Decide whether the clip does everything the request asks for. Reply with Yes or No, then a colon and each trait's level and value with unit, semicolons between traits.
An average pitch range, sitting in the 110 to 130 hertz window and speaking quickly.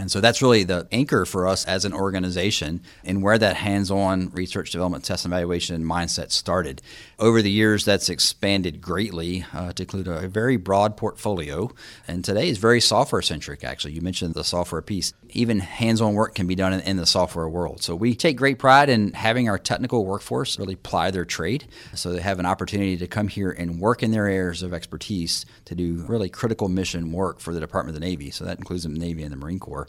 No: average, 3.3 semitones; very low, 95 Hz; fast, 220 wpm